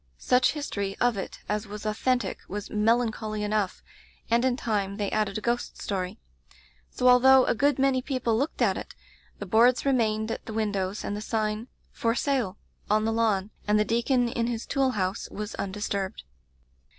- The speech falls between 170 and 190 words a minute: Yes, average, 180 wpm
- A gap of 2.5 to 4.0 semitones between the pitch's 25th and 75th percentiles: Yes, average, 2.9 semitones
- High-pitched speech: Yes, high, 220 Hz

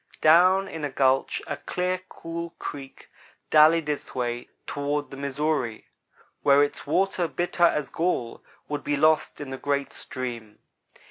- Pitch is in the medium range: Yes, medium, 145 Hz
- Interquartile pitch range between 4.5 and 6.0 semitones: No, average, 3.5 semitones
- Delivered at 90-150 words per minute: Yes, average, 145 wpm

